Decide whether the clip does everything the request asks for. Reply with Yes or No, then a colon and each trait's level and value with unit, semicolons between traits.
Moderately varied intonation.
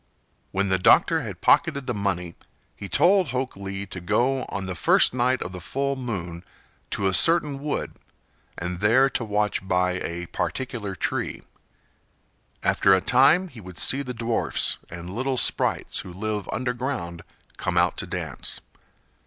No: wide, 6.0 semitones